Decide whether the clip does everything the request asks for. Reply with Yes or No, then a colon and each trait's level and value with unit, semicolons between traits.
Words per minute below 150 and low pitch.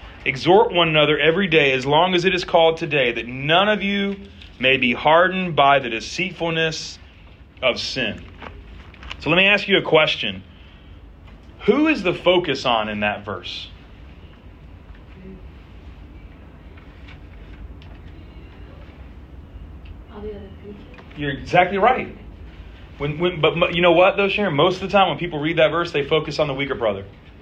Yes: average, 140 wpm; low, 105 Hz